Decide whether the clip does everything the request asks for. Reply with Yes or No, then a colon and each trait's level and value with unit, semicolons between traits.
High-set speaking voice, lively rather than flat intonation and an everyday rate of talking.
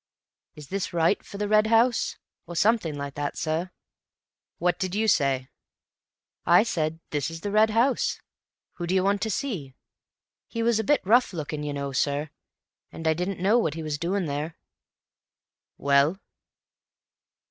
No: medium, 175 Hz; wide, 5.9 semitones; average, 165 wpm